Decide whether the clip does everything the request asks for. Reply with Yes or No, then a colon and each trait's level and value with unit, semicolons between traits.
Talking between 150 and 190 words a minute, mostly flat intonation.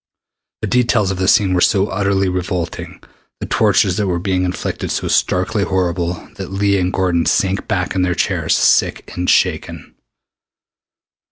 Yes: average, 160 wpm; narrow, 1.6 semitones